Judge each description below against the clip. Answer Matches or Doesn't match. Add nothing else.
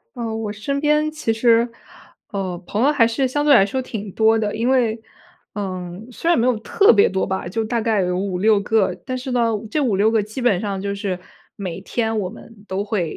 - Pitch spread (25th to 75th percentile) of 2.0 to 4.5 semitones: Matches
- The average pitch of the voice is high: Matches